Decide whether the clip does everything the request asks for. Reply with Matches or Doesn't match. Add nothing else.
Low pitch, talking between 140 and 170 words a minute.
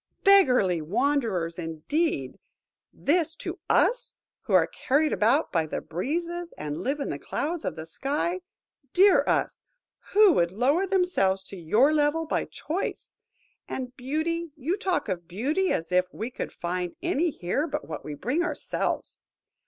Doesn't match